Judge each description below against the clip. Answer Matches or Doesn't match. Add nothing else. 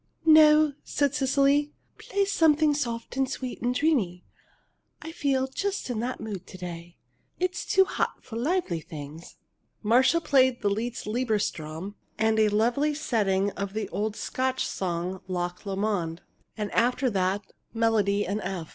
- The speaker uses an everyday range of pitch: Doesn't match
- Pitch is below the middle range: Doesn't match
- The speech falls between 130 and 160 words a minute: Matches